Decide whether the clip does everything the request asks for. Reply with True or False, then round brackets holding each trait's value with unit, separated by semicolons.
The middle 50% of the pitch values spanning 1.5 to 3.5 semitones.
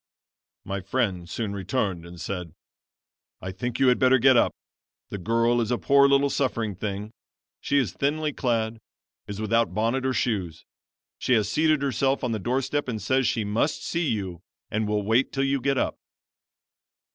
False (4.7 semitones)